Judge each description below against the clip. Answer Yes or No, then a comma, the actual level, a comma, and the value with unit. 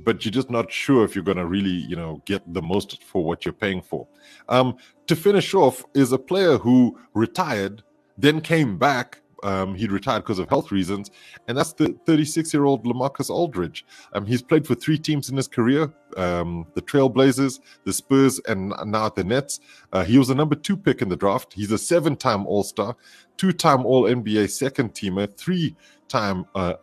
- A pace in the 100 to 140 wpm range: No, average, 185 wpm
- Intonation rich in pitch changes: Yes, wide, 6.2 semitones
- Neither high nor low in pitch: No, low, 125 Hz